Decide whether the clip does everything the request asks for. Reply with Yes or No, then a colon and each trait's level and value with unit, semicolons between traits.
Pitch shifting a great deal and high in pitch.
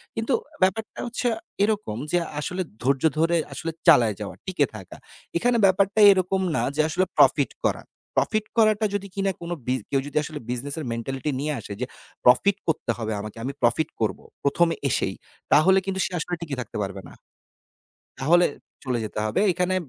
No: wide, 7.0 semitones; medium, 160 Hz